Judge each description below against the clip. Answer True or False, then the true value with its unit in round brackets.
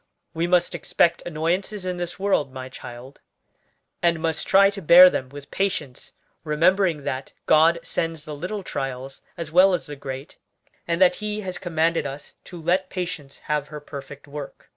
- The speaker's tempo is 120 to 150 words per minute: False (170 wpm)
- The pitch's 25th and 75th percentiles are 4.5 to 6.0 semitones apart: False (4.1 semitones)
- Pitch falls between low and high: True (165 Hz)